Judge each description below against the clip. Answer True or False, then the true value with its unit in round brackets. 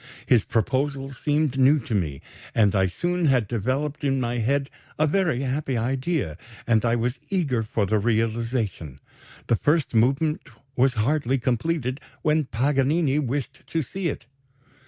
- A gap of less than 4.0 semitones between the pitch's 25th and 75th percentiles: False (4.3 semitones)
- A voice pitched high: False (130 Hz)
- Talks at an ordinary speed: True (150 wpm)